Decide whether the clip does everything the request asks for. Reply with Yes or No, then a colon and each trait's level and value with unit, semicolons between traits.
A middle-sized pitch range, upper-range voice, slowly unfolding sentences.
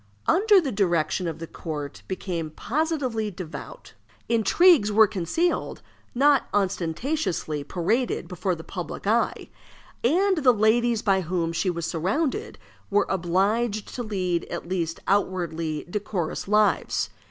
No: wide, 5.8 semitones; high, 200 Hz; slow, 120 wpm